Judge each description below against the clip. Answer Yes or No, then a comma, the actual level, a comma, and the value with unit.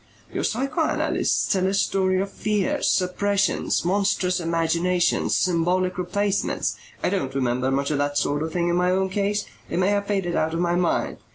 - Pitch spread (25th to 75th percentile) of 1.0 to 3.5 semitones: Yes, average, 2.9 semitones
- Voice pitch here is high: No, medium, 180 Hz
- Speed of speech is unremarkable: Yes, average, 175 wpm